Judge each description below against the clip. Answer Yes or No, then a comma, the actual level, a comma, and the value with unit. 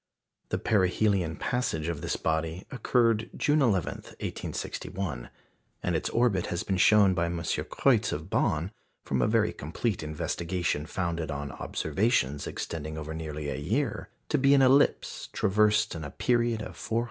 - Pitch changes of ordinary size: No, wide, 5.9 semitones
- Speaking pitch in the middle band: No, very low, 90 Hz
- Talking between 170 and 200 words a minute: No, average, 160 wpm